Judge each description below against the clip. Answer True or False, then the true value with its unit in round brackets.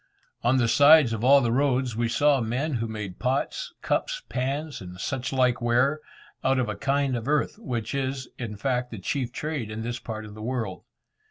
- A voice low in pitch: True (125 Hz)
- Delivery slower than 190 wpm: False (200 wpm)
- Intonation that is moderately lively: True (3.3 semitones)